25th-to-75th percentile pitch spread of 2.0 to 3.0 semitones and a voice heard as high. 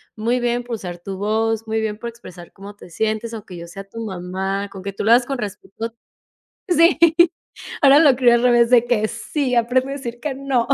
No: average, 3.4 semitones; high, 230 Hz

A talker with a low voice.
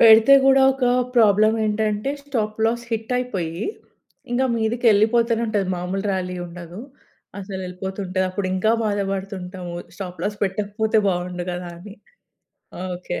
No: high, 205 Hz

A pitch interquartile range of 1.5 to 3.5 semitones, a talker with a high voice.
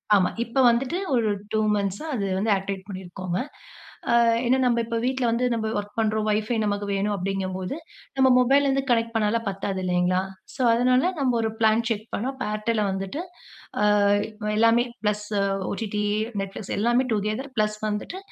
Yes: average, 3.2 semitones; high, 215 Hz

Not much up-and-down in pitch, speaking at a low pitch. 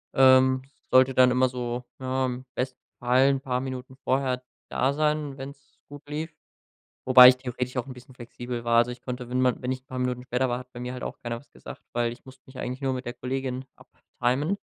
Yes: narrow, 1.1 semitones; low, 130 Hz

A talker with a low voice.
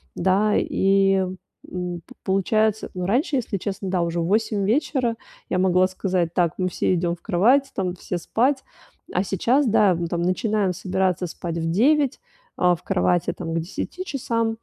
No: high, 190 Hz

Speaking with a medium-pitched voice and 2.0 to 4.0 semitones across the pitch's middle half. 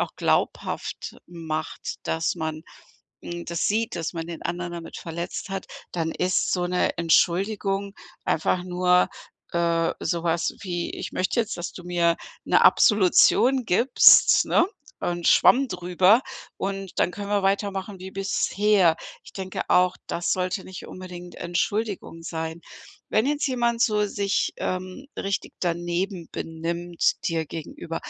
Yes: medium, 180 Hz; narrow, 2.6 semitones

